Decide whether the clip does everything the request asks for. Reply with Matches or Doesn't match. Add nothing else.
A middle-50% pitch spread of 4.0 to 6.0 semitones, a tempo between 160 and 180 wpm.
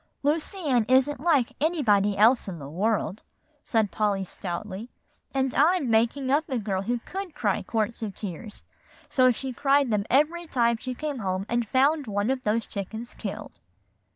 Matches